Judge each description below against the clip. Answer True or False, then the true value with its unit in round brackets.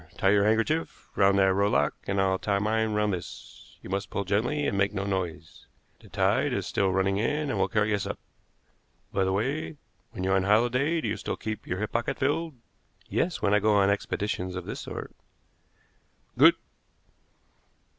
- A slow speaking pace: False (185 wpm)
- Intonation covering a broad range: False (2.8 semitones)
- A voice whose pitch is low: True (100 Hz)